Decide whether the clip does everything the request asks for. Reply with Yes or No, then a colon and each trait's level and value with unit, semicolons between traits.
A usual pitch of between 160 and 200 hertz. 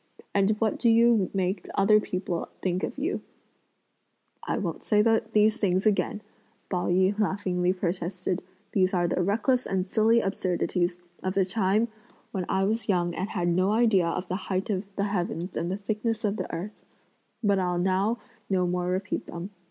Yes: high, 190 Hz